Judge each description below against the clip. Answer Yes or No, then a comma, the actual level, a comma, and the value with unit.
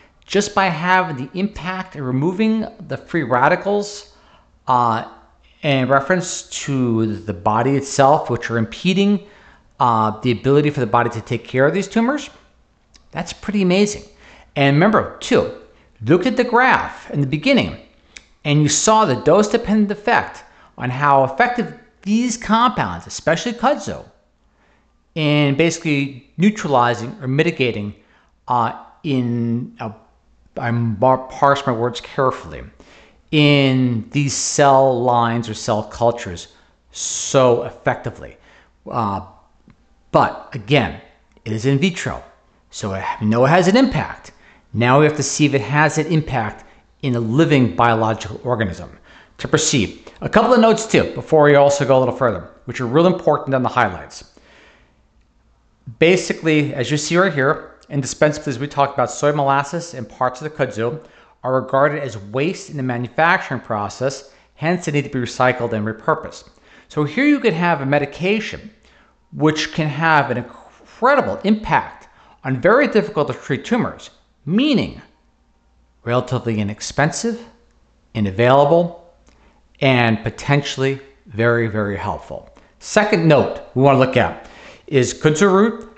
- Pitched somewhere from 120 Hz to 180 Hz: Yes, medium, 140 Hz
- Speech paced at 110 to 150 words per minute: Yes, average, 145 wpm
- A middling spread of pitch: No, wide, 6.2 semitones